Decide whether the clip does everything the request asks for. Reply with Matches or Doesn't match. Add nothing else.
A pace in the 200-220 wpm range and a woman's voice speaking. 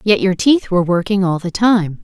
Doesn't match